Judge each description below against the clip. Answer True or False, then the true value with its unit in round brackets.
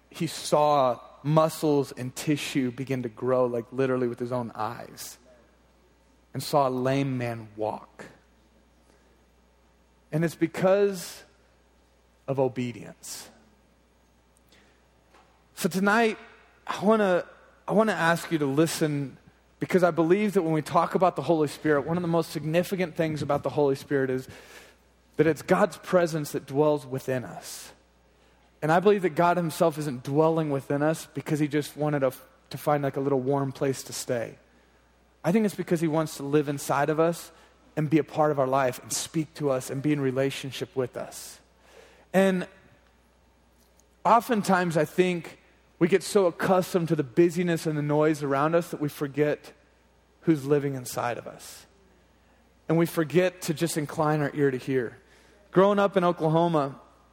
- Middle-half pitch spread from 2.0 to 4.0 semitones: False (4.9 semitones)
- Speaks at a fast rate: False (165 wpm)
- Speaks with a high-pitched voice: False (145 Hz)